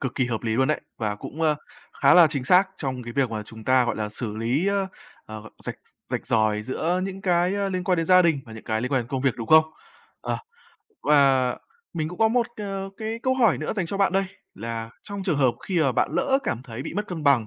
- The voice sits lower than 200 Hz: Yes, medium, 140 Hz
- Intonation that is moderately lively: No, wide, 7.6 semitones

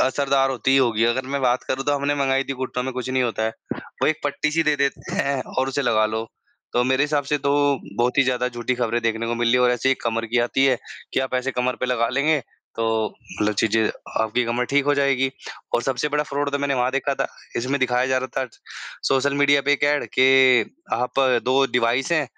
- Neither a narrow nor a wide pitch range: No, narrow, 2.3 semitones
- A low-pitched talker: Yes, low, 130 Hz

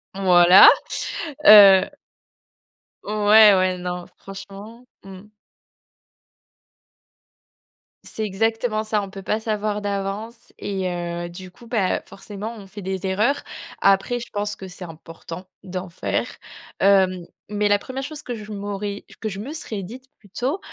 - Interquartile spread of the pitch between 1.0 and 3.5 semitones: Yes, narrow, 2.4 semitones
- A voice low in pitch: No, high, 200 Hz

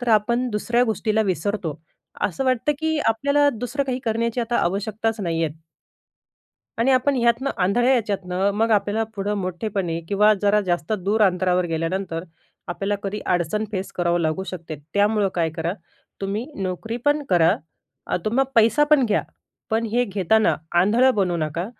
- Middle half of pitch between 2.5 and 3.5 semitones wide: No, average, 4.3 semitones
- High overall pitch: Yes, high, 210 Hz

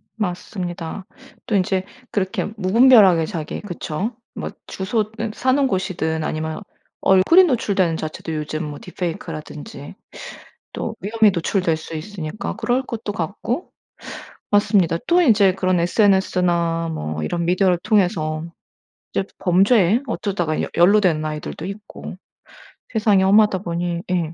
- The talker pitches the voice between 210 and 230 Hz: No, medium, 185 Hz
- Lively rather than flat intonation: No, average, 4.0 semitones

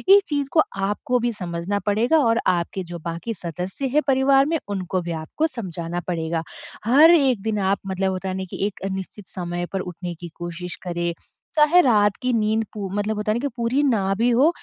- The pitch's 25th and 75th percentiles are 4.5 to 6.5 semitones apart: Yes, wide, 5.6 semitones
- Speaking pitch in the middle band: No, high, 205 Hz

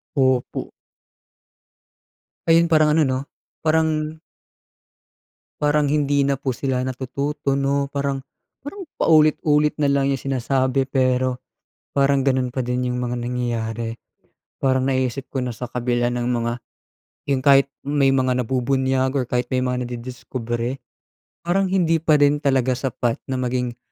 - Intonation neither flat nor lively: No, narrow, 2.2 semitones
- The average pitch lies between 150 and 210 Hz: No, low, 130 Hz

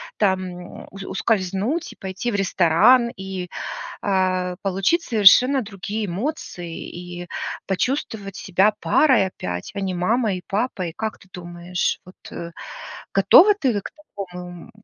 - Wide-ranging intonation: No, average, 3.6 semitones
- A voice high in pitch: Yes, high, 195 Hz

